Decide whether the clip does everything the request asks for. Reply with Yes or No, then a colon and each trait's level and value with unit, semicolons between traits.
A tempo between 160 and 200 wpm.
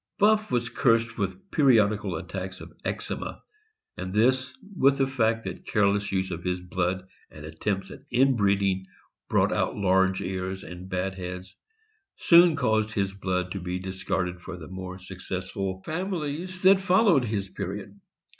No: average, 150 wpm